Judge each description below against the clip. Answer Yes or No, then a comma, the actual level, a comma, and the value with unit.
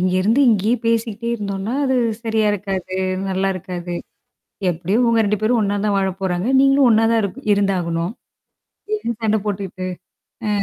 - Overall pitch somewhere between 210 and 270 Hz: No, high, 200 Hz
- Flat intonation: No, average, 3.2 semitones